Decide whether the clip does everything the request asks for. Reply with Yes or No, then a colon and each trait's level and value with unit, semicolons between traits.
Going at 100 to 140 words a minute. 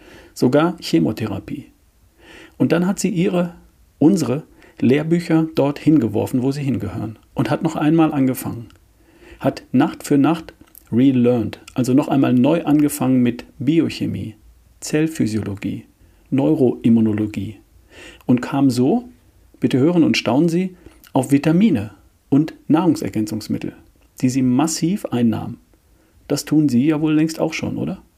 Yes: slow, 125 wpm